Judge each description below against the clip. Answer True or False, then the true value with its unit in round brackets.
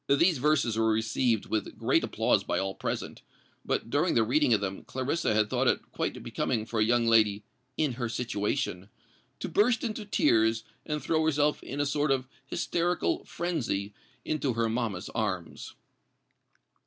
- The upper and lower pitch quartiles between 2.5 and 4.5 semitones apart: False (5.4 semitones)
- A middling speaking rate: True (165 wpm)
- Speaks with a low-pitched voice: True (120 Hz)